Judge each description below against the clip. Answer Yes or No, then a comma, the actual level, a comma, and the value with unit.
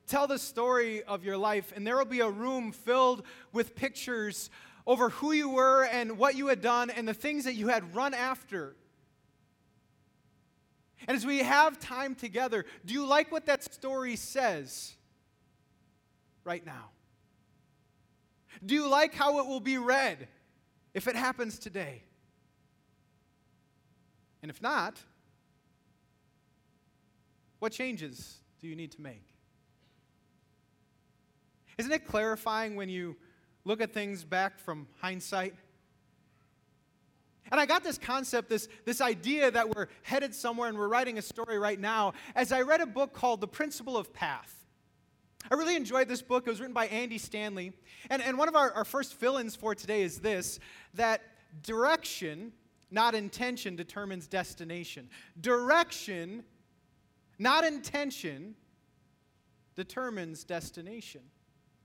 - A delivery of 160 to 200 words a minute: No, average, 140 wpm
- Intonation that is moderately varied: No, wide, 5.9 semitones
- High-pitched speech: Yes, high, 225 Hz